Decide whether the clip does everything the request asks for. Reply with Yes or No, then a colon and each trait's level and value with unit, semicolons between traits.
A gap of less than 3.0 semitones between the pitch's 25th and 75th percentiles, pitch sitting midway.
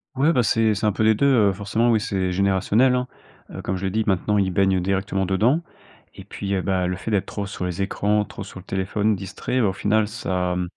No: narrow, 2.4 semitones; low, 100 Hz